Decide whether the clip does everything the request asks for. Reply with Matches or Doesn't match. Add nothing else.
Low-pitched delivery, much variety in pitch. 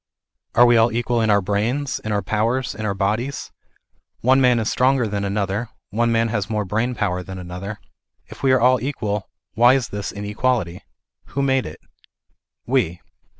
Doesn't match